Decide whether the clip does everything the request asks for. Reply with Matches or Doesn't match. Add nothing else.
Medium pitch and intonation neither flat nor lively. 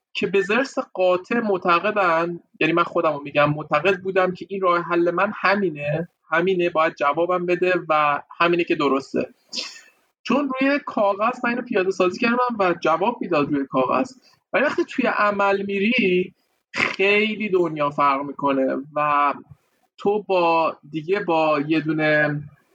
Matches